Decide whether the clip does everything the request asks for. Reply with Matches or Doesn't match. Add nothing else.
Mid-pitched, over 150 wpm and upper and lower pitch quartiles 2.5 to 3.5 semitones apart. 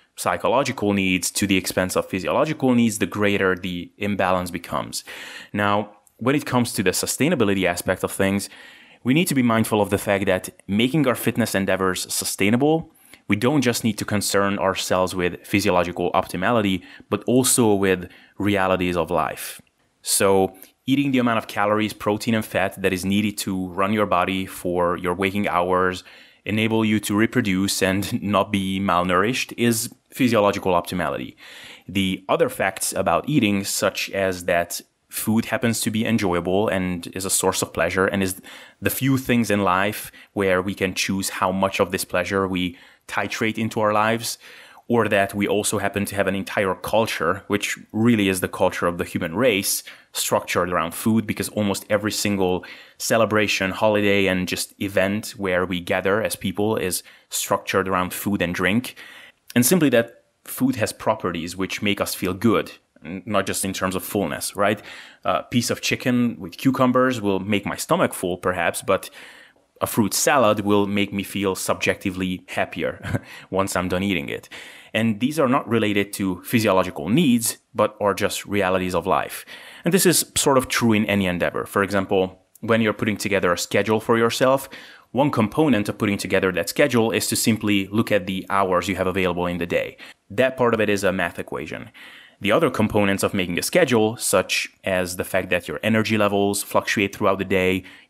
Doesn't match